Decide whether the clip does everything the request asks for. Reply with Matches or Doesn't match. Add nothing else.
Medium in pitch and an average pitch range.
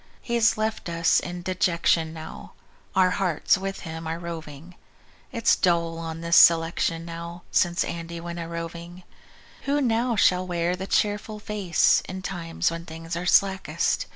Doesn't match